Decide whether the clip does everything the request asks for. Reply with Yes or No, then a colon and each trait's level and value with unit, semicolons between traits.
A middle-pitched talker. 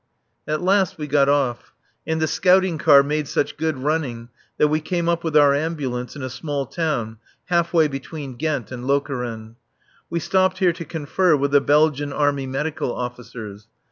Yes: medium, 145 Hz